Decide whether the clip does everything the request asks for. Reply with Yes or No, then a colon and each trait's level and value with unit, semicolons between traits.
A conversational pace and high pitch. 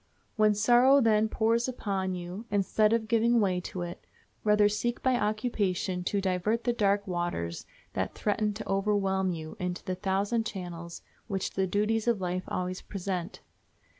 Yes: average, 160 wpm; high, 200 Hz